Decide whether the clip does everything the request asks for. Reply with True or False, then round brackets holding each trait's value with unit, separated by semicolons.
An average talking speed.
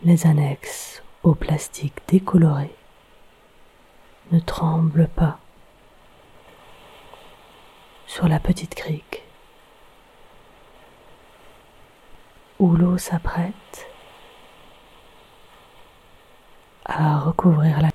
False (60 wpm)